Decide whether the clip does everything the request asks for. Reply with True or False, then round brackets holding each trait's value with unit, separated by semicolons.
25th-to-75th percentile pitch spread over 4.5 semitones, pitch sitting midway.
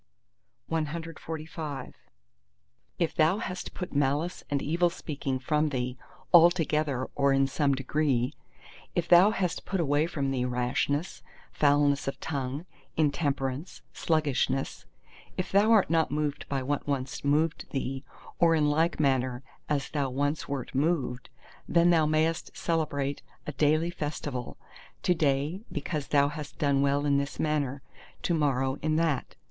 False (2.9 semitones; 145 Hz)